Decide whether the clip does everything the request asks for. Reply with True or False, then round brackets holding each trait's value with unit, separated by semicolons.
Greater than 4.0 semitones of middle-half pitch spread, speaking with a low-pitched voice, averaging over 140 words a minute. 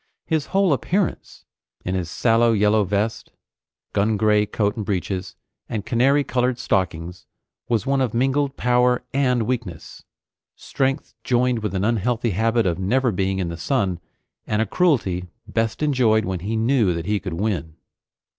True (4.6 semitones; 110 Hz; 155 wpm)